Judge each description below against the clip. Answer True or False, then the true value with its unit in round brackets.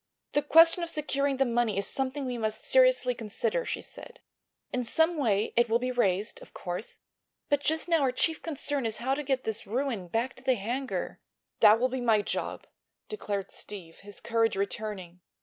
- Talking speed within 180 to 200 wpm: True (190 wpm)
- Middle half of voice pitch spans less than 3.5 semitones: False (4.9 semitones)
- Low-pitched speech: False (245 Hz)